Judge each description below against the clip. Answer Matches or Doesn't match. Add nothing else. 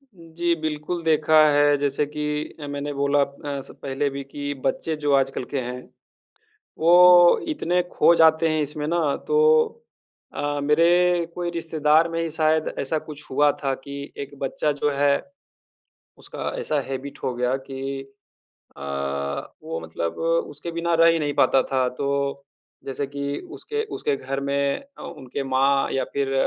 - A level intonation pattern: Doesn't match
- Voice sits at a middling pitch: Matches